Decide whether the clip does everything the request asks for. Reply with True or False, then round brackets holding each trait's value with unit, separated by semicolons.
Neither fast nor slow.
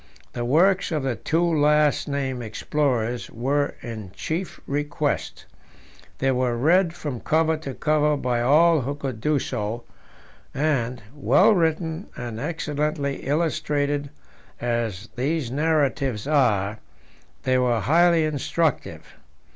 False (120 wpm)